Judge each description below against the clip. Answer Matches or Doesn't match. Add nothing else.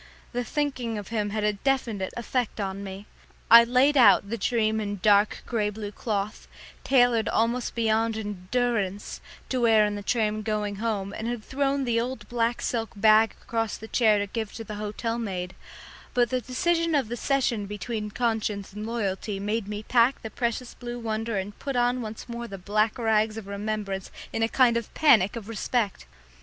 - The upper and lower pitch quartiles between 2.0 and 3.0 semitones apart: Matches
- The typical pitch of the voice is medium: Doesn't match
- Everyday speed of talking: Matches